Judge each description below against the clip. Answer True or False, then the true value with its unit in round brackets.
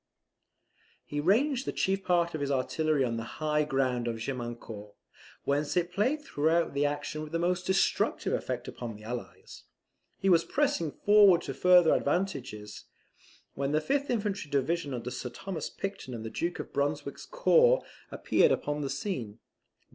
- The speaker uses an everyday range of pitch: False (6.2 semitones)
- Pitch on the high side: False (155 Hz)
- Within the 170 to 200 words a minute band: False (160 wpm)